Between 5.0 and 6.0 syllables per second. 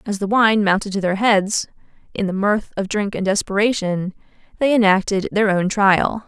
No: 4.8 syllables/s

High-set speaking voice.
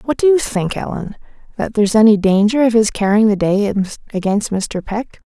Yes: high, 215 Hz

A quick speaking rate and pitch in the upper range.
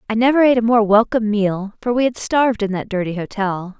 Yes: fast, 235 wpm; high, 220 Hz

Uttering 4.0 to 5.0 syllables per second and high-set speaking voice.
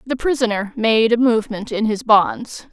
Yes: 4.7 syllables/s; high, 225 Hz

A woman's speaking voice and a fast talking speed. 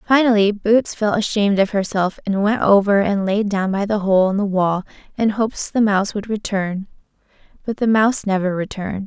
No: female; average, 190 wpm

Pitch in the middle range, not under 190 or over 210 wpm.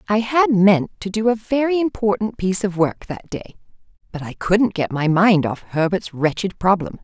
No: high, 200 Hz; average, 195 wpm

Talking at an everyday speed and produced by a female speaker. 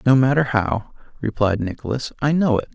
No: average, 175 wpm; male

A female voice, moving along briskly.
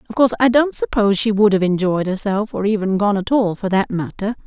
Yes: female; fast, 230 wpm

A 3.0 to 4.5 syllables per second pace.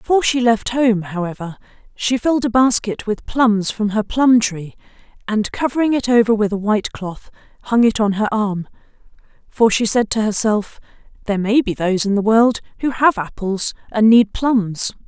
No: 5.0 syllables/s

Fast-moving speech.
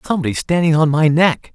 No: average, 195 wpm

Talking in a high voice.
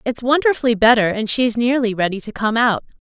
Yes: high, 235 Hz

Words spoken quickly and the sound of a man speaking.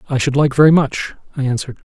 Yes: fast, 220 wpm; male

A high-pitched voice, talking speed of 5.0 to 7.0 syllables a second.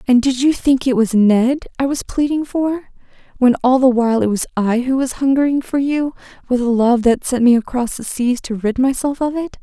Yes: very high, 255 Hz; 5.2 syllables/s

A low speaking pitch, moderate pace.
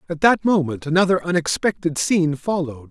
No: medium, 165 Hz; average, 145 wpm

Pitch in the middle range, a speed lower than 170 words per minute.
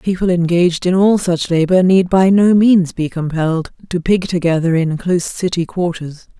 No: medium, 175 Hz; average, 180 wpm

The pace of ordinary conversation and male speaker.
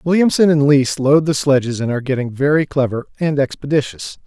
Yes: average, 185 wpm; male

